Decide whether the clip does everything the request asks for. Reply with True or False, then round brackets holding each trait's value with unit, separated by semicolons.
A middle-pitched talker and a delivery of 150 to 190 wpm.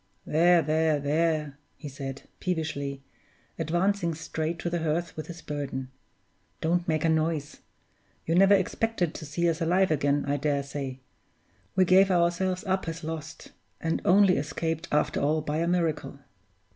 True (160 Hz; 155 wpm)